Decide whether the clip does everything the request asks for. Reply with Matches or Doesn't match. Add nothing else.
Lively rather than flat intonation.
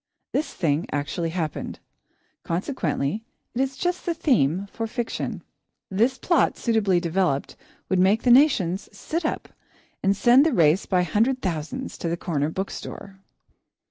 Matches